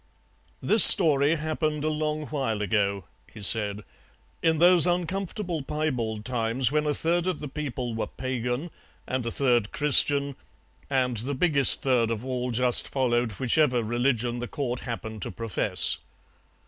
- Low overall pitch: Yes, low, 130 Hz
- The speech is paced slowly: No, average, 150 wpm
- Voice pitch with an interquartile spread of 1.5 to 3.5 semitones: No, average, 4.4 semitones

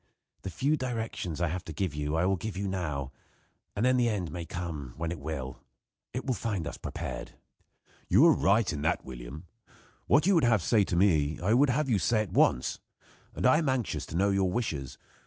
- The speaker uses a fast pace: Yes, fast, 215 wpm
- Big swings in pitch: Yes, wide, 6.8 semitones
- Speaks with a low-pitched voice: Yes, very low, 95 Hz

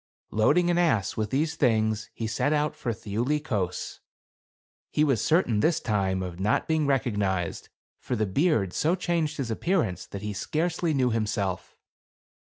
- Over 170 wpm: No, average, 165 wpm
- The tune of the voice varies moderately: No, wide, 7.0 semitones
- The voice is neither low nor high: No, low, 115 Hz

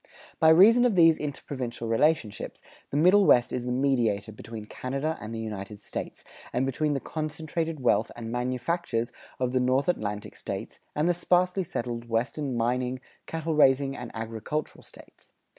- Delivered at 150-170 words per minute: Yes, average, 160 wpm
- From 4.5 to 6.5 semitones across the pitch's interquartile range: Yes, average, 5.2 semitones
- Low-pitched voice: Yes, low, 130 Hz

